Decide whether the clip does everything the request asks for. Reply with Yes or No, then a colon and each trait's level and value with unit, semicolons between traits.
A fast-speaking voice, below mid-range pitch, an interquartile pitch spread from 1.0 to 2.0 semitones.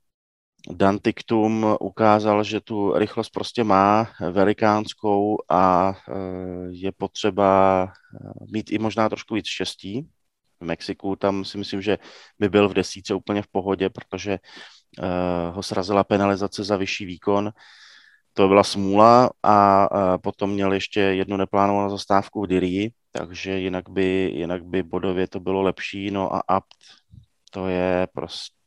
No: average, 140 wpm; low, 100 Hz; narrow, 1.7 semitones